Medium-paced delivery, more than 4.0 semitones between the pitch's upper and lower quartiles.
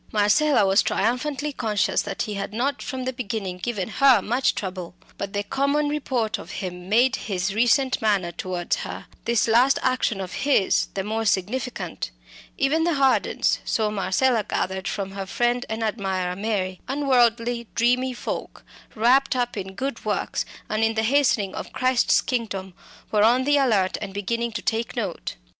Yes: average, 165 wpm; average, 4.6 semitones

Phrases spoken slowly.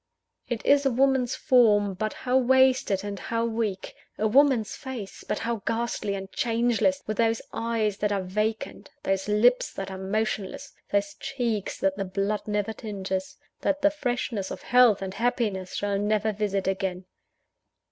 No: average, 160 wpm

